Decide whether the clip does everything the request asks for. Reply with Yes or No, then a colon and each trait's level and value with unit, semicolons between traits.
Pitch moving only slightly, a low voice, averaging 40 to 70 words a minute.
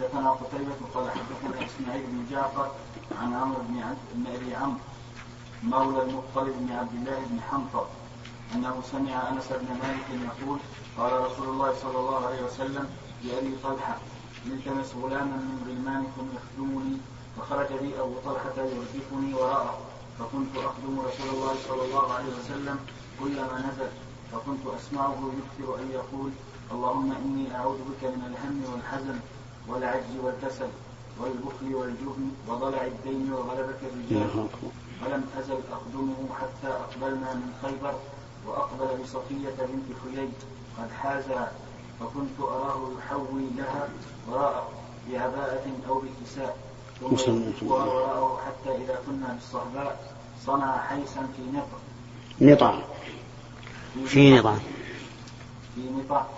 No: narrow, 1.4 semitones; low, 130 Hz; average, 115 wpm